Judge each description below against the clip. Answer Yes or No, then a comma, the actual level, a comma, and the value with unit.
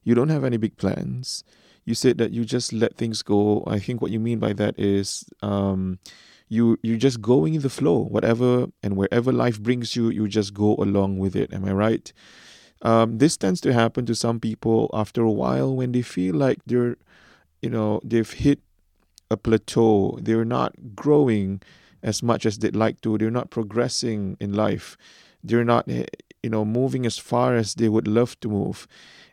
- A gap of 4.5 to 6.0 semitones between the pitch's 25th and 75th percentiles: No, narrow, 2.5 semitones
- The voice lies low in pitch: Yes, low, 115 Hz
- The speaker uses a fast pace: No, average, 190 wpm